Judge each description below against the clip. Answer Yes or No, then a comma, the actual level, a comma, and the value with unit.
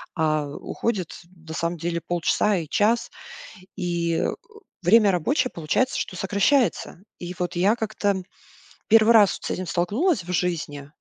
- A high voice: No, medium, 180 Hz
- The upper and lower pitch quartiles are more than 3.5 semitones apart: Yes, average, 4.0 semitones